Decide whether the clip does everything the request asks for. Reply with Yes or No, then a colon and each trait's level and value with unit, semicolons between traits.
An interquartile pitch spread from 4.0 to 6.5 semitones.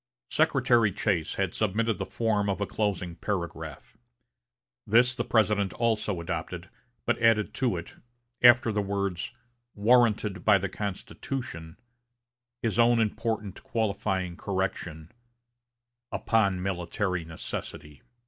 No: average, 3.6 semitones